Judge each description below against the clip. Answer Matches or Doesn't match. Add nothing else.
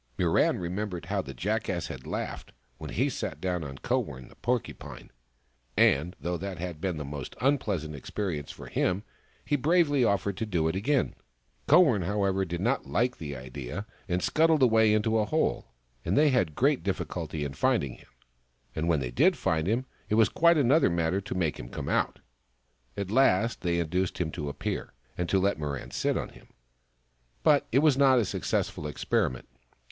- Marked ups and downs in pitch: Matches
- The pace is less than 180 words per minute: Doesn't match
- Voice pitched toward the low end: Matches